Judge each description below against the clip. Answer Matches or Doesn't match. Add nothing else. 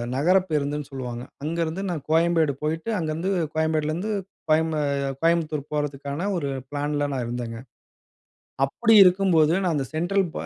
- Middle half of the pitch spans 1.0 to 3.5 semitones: Matches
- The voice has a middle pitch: Matches